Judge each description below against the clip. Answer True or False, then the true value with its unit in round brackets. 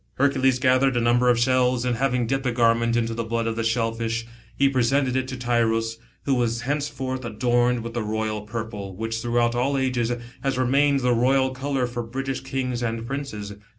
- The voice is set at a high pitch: False (120 Hz)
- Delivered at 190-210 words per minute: True (195 wpm)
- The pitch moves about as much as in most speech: False (2.2 semitones)